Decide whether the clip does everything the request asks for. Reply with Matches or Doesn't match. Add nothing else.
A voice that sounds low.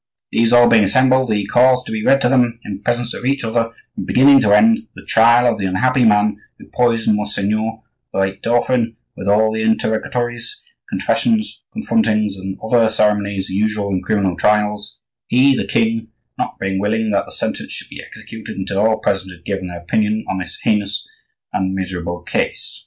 Matches